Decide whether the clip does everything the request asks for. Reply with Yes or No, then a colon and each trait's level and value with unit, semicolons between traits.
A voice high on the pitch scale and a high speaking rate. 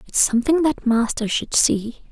No: very high, 250 Hz; average, 170 wpm